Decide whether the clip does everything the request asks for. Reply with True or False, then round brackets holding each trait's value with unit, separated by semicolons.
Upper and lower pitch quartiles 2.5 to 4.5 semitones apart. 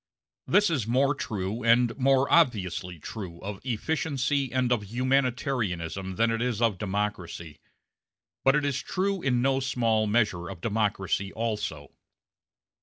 False (5.0 semitones)